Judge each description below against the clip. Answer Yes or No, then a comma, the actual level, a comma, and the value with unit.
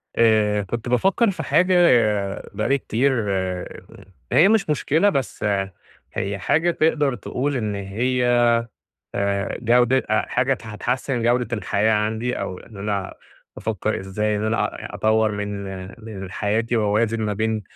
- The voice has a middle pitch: No, low, 110 Hz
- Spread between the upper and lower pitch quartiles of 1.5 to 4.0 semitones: Yes, average, 3.6 semitones